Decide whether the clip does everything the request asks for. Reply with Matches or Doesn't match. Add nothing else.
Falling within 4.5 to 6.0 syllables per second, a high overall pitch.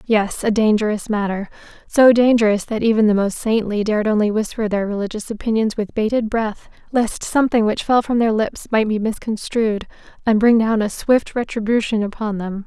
Matches